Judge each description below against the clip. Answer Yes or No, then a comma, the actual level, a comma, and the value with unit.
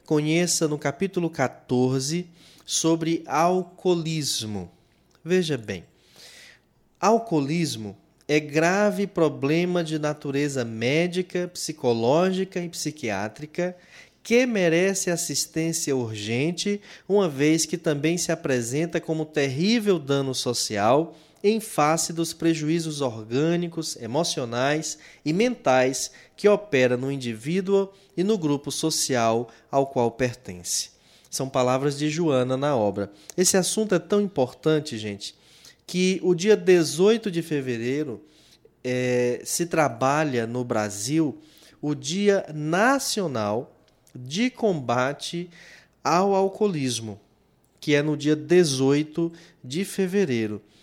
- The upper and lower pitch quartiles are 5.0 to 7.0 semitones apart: Yes, wide, 5.5 semitones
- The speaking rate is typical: No, slow, 105 wpm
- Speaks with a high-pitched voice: No, medium, 155 Hz